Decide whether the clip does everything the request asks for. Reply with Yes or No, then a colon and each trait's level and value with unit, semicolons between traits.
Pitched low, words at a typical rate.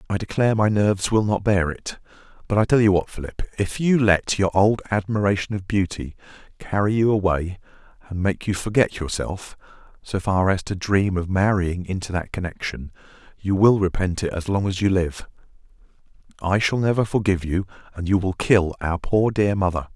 Yes: very low, 95 Hz; average, 185 wpm